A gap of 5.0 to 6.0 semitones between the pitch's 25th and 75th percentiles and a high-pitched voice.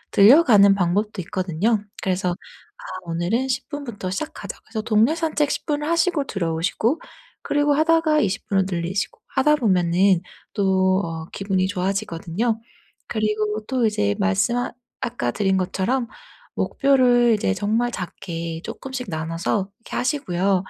Yes: wide, 5.6 semitones; high, 205 Hz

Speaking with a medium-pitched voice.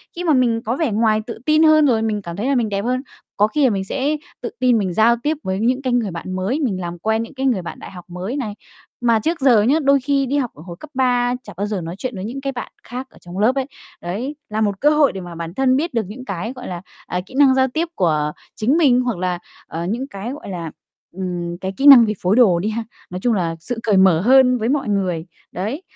No: high, 225 Hz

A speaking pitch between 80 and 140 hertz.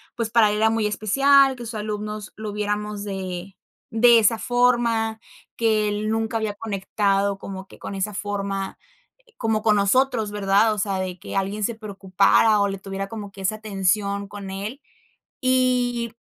No: high, 210 Hz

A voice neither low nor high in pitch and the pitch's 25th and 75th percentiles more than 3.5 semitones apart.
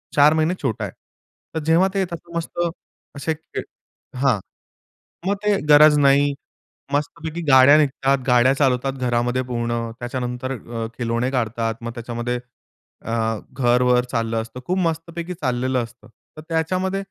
No: low, 130 Hz; average, 4.8 semitones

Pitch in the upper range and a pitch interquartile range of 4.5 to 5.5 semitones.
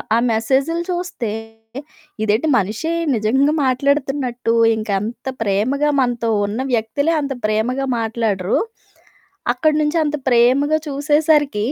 Yes: very high, 255 Hz; average, 4.9 semitones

